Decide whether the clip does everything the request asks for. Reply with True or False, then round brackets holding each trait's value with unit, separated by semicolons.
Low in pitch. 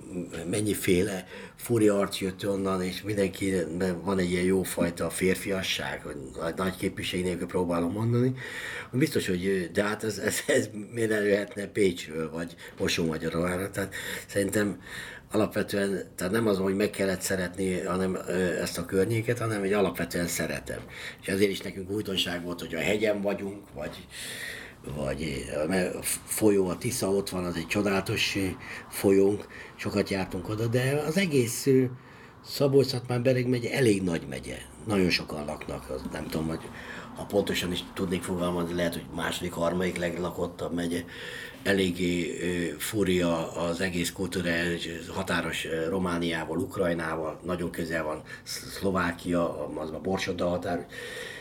True (95 Hz)